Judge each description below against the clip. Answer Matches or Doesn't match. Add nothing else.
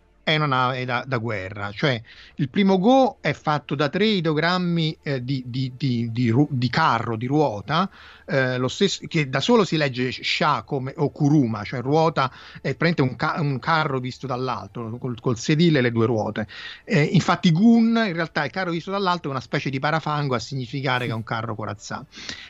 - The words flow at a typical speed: Doesn't match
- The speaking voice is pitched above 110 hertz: Matches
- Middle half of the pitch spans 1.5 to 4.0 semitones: Doesn't match